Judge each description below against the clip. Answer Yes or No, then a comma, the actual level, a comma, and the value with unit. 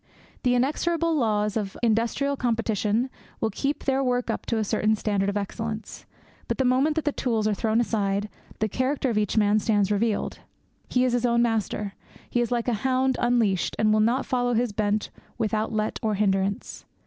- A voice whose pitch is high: Yes, high, 225 Hz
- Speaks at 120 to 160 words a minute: No, average, 190 wpm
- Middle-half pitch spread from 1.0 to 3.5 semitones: Yes, average, 2.8 semitones